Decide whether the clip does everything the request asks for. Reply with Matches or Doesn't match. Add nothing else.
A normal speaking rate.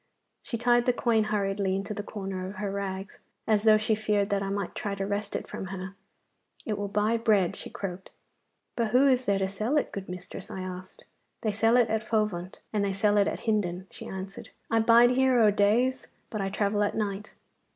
Doesn't match